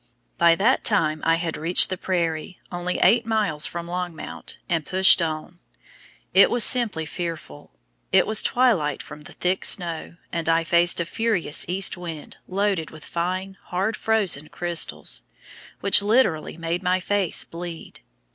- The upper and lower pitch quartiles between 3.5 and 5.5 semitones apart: No, average, 2.9 semitones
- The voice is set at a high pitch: No, medium, 175 Hz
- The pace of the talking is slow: No, average, 150 wpm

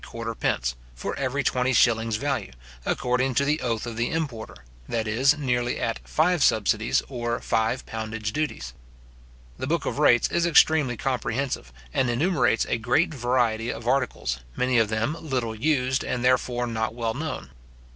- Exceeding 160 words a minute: No, average, 155 wpm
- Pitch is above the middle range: No, low, 125 Hz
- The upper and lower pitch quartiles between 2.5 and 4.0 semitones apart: Yes, average, 3.4 semitones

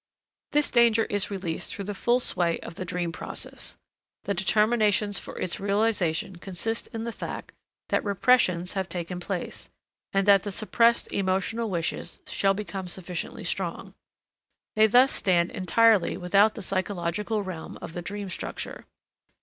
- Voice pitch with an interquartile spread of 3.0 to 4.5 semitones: Yes, average, 3.3 semitones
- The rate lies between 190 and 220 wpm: No, average, 150 wpm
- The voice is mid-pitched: No, high, 195 Hz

